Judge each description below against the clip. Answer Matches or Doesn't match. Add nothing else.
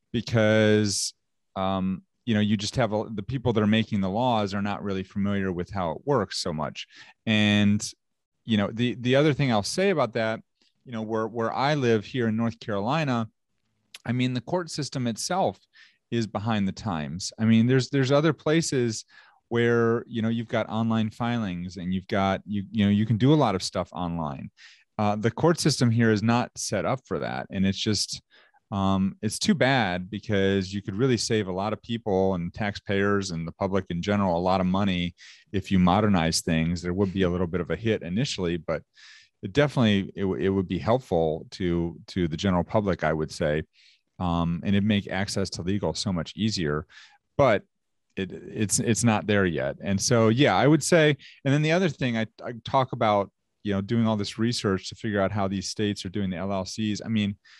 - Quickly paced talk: Matches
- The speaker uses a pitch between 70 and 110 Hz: Matches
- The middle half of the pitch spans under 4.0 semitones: Matches